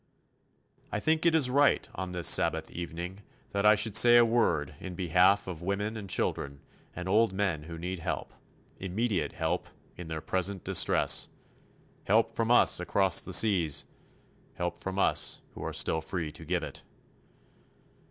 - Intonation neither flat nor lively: Yes, average, 4.0 semitones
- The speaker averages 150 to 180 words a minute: Yes, average, 160 wpm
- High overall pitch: No, very low, 95 Hz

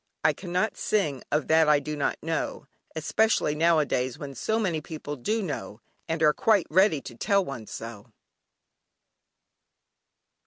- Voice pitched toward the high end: No, medium, 155 Hz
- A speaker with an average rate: Yes, average, 145 wpm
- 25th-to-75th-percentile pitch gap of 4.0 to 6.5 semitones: Yes, average, 4.6 semitones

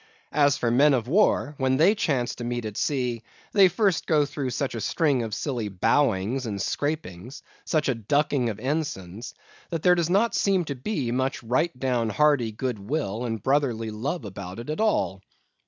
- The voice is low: Yes, low, 130 Hz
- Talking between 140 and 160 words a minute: No, average, 190 wpm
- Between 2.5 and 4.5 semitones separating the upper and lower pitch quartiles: No, average, 4.9 semitones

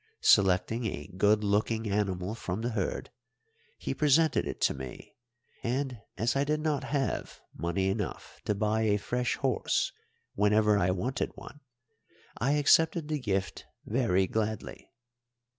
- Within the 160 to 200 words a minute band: No, average, 140 wpm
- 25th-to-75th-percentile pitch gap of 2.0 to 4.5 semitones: No, average, 5.0 semitones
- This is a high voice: No, low, 110 Hz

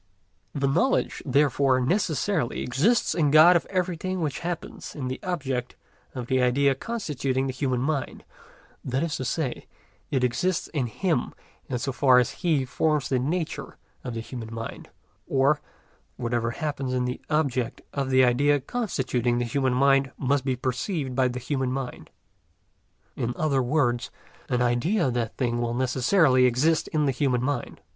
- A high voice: No, low, 135 Hz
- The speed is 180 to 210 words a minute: No, average, 165 wpm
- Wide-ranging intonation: No, average, 3.4 semitones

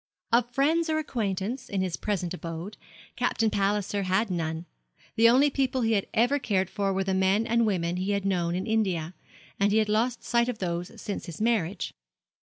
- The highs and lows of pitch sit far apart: No, average, 3.8 semitones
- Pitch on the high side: Yes, high, 205 Hz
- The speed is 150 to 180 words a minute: No, average, 190 wpm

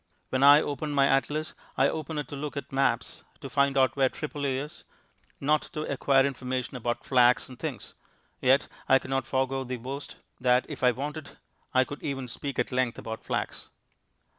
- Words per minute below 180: No, average, 185 wpm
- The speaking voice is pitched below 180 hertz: Yes, low, 135 Hz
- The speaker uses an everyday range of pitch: No, narrow, 1.8 semitones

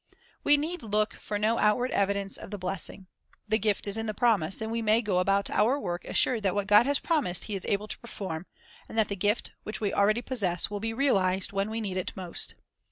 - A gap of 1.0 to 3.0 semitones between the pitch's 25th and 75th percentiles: Yes, narrow, 2.5 semitones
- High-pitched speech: Yes, high, 210 Hz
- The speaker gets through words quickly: Yes, fast, 235 wpm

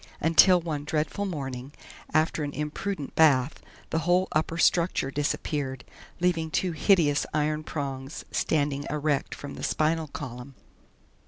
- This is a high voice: No, medium, 150 Hz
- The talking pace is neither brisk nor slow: No, slow, 130 wpm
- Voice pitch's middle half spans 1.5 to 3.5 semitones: Yes, narrow, 2.4 semitones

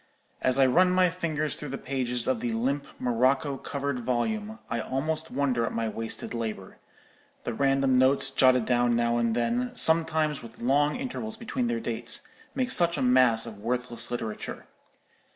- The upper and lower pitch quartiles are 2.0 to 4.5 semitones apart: No, average, 5.0 semitones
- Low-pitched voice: Yes, low, 130 Hz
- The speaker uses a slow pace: No, average, 165 wpm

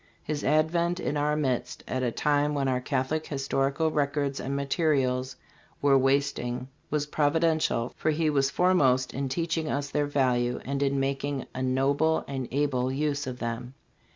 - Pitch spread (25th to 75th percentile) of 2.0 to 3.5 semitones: Yes, narrow, 2.4 semitones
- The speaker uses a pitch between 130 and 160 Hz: Yes, medium, 140 Hz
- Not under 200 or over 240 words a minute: No, average, 165 wpm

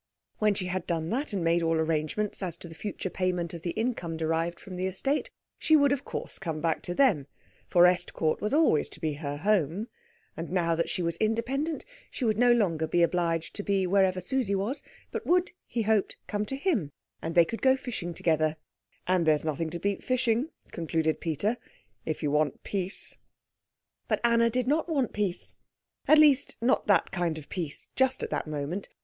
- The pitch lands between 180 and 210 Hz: Yes, medium, 185 Hz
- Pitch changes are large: Yes, wide, 6.0 semitones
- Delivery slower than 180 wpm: No, average, 200 wpm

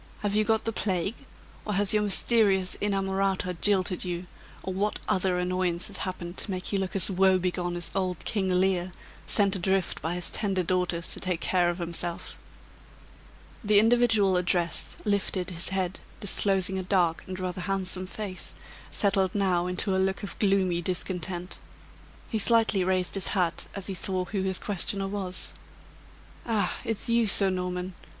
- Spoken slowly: No, average, 165 wpm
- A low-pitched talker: No, high, 190 Hz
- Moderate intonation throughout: No, narrow, 1.7 semitones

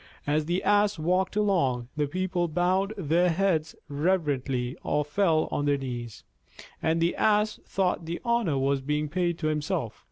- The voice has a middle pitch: Yes, medium, 160 Hz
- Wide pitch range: No, average, 4.3 semitones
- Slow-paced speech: No, average, 160 wpm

